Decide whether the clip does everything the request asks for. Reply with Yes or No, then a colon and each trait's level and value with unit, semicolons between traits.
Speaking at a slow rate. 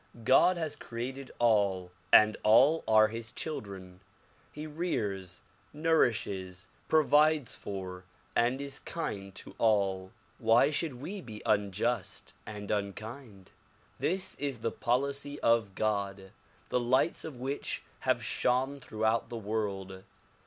Yes: slow, 125 wpm